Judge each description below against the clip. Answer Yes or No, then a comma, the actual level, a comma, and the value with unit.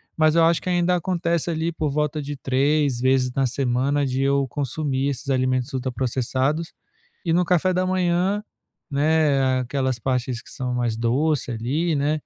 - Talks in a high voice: No, medium, 140 Hz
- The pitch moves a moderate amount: Yes, average, 3.9 semitones